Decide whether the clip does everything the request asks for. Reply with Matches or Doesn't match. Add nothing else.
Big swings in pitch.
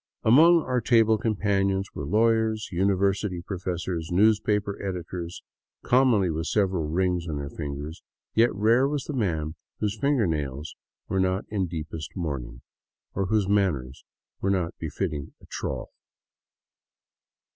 Doesn't match